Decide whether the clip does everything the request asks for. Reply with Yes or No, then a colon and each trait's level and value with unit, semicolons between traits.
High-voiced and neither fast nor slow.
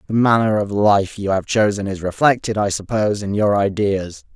No: low, 100 Hz; average, 195 wpm